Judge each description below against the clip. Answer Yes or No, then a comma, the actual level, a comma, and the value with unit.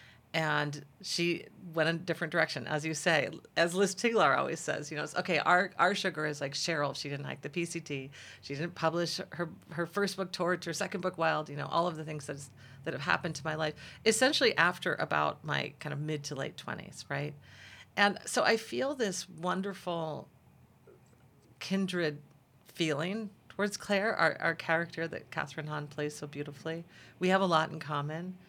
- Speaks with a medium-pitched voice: Yes, medium, 160 Hz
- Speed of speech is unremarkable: Yes, average, 190 wpm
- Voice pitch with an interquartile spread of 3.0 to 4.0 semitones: Yes, average, 3.6 semitones